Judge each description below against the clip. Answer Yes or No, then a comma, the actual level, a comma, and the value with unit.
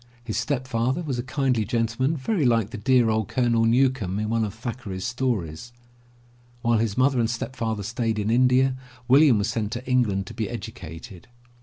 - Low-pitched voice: Yes, low, 120 Hz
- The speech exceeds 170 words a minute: Yes, average, 180 wpm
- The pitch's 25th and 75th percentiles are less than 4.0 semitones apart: Yes, average, 2.9 semitones